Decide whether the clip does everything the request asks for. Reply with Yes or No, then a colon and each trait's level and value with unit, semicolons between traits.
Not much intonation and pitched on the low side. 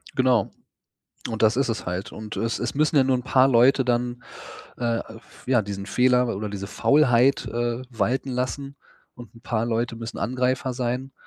Yes: narrow, 2.1 semitones; low, 120 Hz